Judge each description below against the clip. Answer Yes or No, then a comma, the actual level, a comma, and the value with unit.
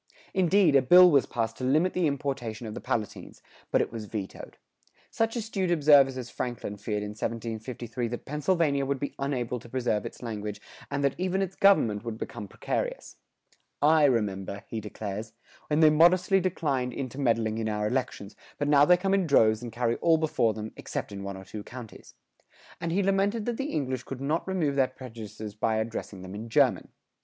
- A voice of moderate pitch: No, low, 130 Hz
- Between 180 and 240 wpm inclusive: Yes, average, 190 wpm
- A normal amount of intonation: No, wide, 6.3 semitones